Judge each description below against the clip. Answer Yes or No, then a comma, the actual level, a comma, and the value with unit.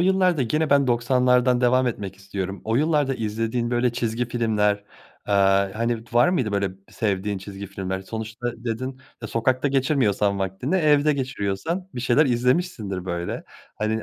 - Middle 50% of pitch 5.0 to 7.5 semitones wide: No, average, 4.3 semitones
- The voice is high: No, low, 120 Hz